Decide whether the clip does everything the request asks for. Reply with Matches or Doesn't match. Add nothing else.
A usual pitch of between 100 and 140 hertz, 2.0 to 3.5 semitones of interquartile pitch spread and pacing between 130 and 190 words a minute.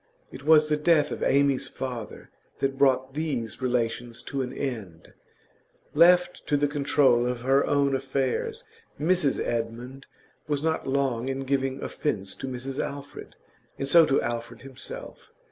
Matches